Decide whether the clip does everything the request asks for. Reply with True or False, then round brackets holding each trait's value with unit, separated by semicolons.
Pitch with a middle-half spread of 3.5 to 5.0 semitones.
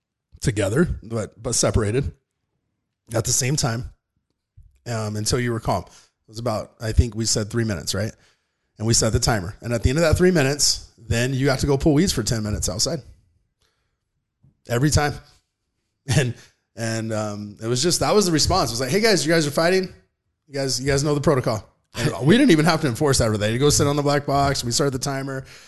True (4.7 semitones)